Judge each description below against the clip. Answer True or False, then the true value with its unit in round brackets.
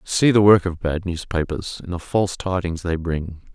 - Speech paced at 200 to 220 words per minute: True (205 wpm)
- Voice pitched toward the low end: True (90 Hz)